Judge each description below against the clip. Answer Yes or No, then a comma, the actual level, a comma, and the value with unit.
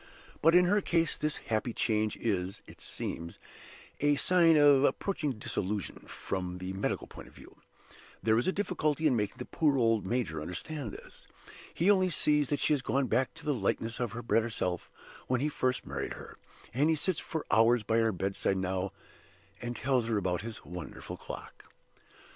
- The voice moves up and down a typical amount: No, wide, 6.4 semitones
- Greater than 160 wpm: Yes, average, 185 wpm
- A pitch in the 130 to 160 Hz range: No, low, 120 Hz